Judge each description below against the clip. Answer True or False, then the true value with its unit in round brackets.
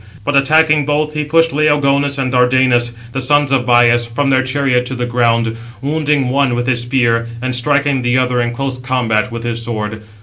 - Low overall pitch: True (130 Hz)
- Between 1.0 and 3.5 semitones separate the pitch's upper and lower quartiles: True (2.9 semitones)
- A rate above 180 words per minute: True (195 wpm)